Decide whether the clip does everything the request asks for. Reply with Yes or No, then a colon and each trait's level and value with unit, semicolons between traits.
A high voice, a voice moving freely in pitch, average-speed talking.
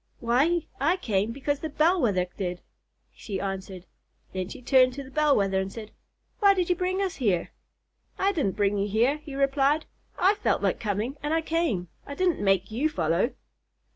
Yes: very high, 260 Hz; wide, 8.0 semitones; average, 190 wpm